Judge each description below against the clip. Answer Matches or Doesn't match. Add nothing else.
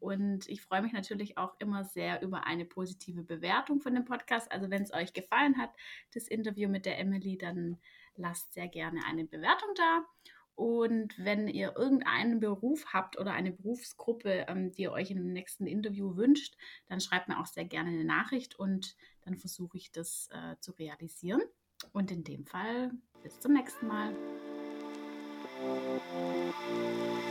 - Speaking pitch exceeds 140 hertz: Matches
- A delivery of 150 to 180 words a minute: Matches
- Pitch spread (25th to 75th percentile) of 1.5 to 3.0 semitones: Doesn't match